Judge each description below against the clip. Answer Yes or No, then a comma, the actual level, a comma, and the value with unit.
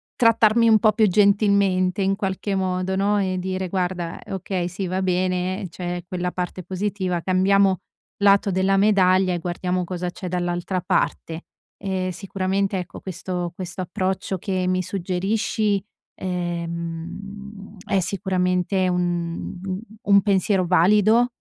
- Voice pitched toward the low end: No, medium, 185 Hz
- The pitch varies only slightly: Yes, narrow, 1.8 semitones